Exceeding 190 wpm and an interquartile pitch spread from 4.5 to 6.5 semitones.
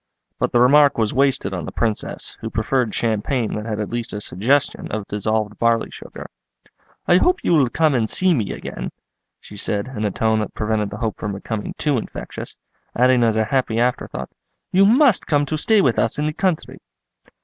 Yes: average, 200 wpm; average, 4.9 semitones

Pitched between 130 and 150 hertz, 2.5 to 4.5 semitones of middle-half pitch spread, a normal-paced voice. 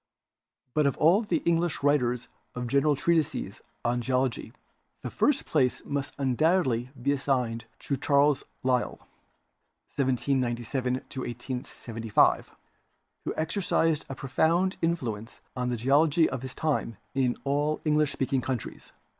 No: low, 135 Hz; average, 3.5 semitones; slow, 125 wpm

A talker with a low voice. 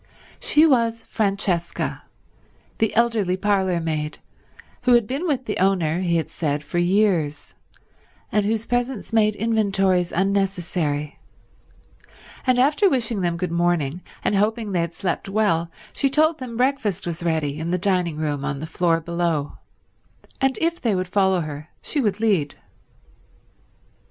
No: high, 190 Hz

